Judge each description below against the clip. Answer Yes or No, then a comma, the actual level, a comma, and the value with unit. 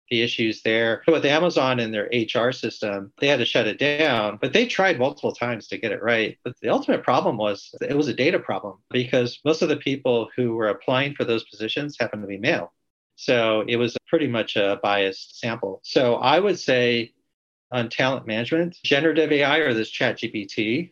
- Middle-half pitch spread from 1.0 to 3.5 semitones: No, average, 4.7 semitones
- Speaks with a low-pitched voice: Yes, low, 120 Hz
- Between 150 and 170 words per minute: No, fast, 205 wpm